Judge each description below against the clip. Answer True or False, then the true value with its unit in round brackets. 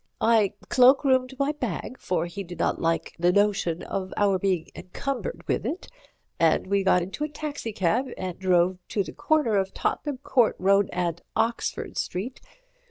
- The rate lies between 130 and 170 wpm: True (165 wpm)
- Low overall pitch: False (200 Hz)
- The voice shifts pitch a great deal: True (6.1 semitones)